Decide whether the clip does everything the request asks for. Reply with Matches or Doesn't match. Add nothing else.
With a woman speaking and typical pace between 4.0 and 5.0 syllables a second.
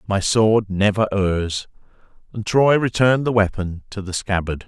Doesn't match